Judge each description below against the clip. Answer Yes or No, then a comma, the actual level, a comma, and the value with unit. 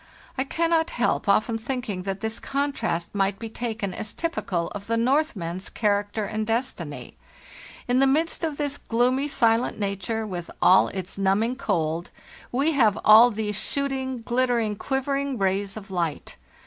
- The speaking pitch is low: No, high, 225 Hz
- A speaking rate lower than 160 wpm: Yes, average, 150 wpm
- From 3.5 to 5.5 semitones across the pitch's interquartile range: Yes, average, 5.0 semitones